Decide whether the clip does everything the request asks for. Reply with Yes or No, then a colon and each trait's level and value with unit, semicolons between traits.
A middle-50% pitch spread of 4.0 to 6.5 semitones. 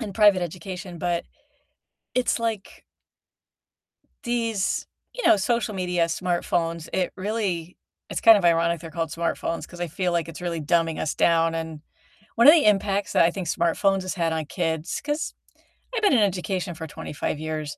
No: average, 3.3 semitones